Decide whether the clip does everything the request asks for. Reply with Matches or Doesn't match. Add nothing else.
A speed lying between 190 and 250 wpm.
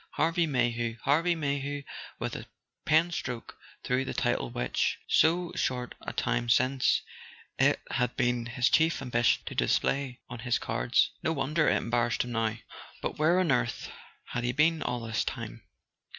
Doesn't match